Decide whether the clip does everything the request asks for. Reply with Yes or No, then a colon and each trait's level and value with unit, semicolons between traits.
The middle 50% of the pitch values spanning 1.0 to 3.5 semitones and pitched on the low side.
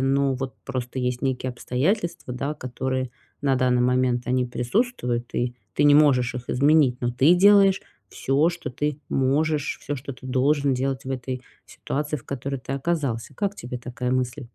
Yes: average, 2.8 semitones; low, 130 Hz